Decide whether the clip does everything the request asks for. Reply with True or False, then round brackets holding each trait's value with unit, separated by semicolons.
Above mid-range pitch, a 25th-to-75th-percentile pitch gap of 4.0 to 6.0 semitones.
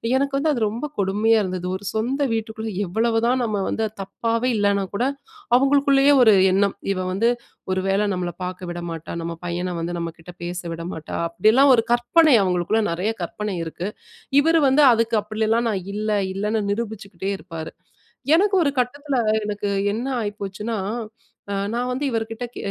True (215 Hz; 4.3 semitones)